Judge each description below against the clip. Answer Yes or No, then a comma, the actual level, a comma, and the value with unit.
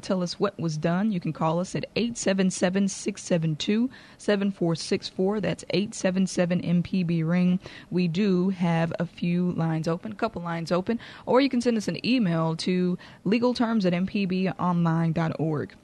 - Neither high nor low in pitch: Yes, medium, 180 Hz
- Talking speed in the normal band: Yes, average, 150 wpm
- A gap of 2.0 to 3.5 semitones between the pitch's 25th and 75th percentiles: Yes, average, 3.2 semitones